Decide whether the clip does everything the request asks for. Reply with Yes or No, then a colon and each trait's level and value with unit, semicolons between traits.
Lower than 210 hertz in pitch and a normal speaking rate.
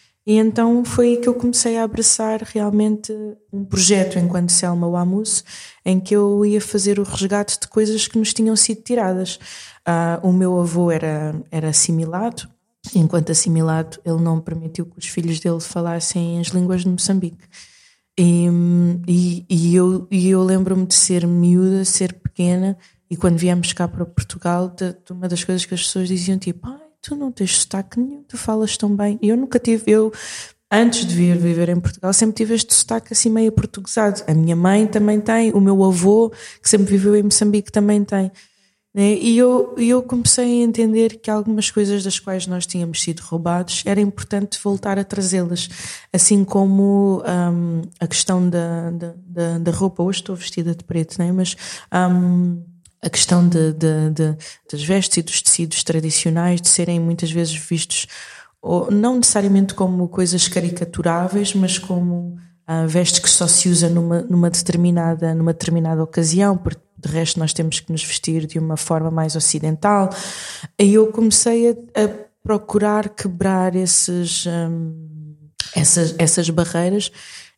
Yes: medium, 185 Hz; average, 170 wpm